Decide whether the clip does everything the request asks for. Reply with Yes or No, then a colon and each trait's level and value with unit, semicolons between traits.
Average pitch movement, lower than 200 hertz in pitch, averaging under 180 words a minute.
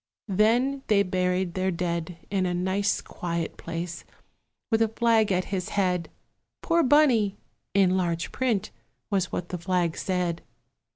Yes: average, 3.2 semitones; medium, 185 Hz; average, 140 wpm